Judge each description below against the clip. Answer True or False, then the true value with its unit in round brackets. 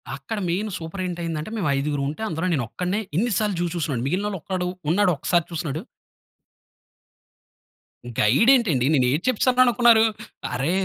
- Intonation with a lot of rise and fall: True (5.7 semitones)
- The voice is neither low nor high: True (175 Hz)